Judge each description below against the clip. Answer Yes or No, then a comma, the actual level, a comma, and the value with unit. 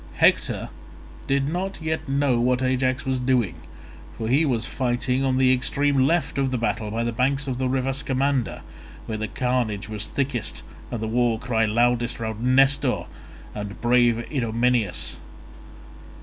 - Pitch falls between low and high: No, low, 125 Hz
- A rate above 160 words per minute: No, average, 155 wpm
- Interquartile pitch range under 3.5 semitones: Yes, narrow, 2.6 semitones